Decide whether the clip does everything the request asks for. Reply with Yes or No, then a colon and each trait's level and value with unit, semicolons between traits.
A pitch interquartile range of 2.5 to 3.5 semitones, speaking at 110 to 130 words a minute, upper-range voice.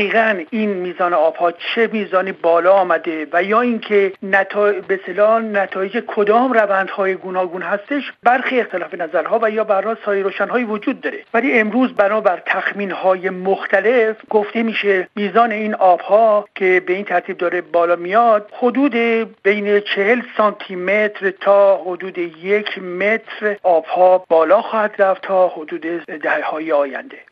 No: average, 3.1 semitones; average, 140 wpm; high, 200 Hz